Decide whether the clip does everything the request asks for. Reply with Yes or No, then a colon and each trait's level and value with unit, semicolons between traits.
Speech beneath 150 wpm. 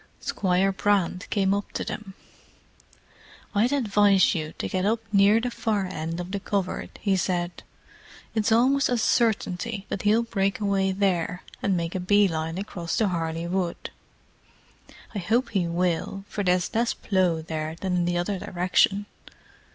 No: average, 160 wpm